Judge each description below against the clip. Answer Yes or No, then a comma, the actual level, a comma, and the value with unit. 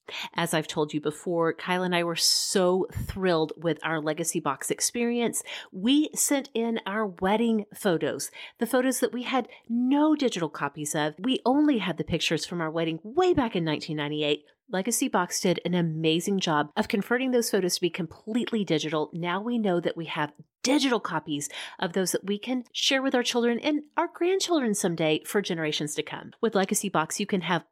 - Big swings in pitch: Yes, wide, 6.8 semitones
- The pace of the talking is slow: No, average, 190 wpm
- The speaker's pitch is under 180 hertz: No, medium, 185 Hz